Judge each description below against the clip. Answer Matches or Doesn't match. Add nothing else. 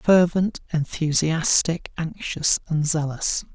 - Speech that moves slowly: Matches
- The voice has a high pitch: Doesn't match